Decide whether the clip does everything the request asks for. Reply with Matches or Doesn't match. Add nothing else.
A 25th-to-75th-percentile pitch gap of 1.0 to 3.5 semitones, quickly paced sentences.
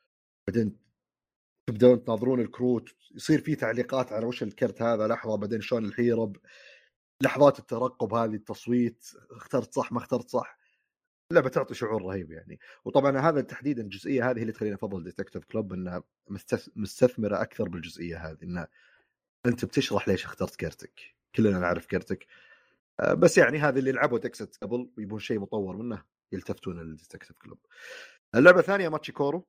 Doesn't match